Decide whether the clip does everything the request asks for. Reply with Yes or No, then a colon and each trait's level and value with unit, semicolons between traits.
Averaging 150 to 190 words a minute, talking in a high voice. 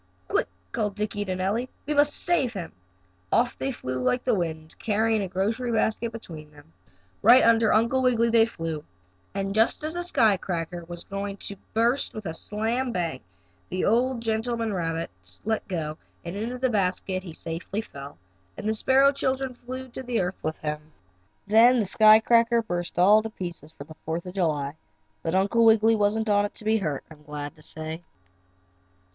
Yes: average, 180 wpm; high, 210 Hz